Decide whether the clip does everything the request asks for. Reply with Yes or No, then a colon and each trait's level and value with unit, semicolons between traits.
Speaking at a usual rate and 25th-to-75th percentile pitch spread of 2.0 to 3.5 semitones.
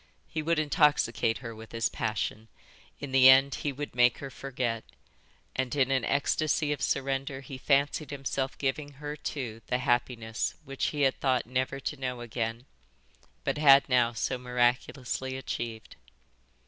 Yes: average, 155 wpm; narrow, 2.5 semitones